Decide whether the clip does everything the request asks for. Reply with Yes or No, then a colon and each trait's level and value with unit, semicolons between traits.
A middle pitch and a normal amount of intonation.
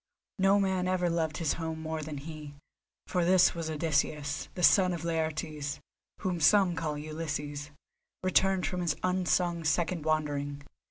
Yes: medium, 160 Hz; average, 3.2 semitones